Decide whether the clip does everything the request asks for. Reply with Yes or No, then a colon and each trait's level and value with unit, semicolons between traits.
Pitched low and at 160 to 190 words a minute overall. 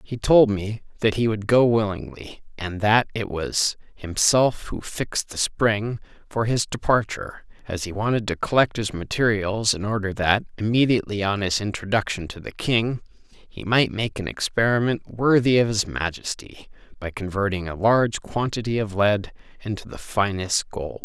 Yes: low, 105 Hz; average, 165 wpm